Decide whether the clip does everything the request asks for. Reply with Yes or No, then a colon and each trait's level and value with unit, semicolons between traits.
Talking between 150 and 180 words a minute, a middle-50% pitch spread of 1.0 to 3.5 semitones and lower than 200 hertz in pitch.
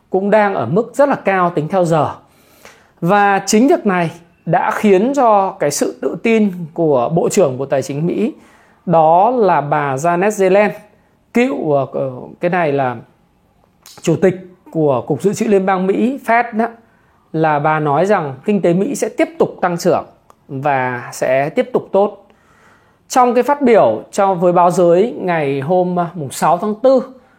No: average, 170 wpm; average, 4.9 semitones; medium, 185 Hz